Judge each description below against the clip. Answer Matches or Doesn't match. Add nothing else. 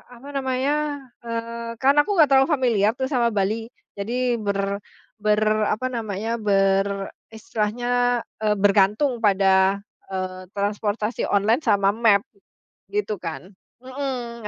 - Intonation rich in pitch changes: Doesn't match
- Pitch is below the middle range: Doesn't match